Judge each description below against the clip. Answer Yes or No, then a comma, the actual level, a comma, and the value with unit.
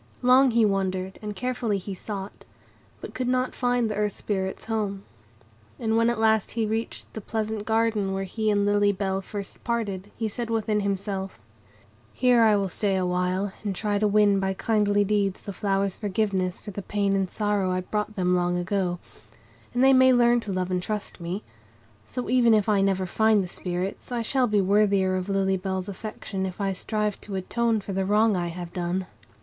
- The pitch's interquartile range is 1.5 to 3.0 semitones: Yes, narrow, 2.5 semitones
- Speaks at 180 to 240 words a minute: Yes, average, 195 wpm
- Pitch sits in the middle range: No, high, 205 Hz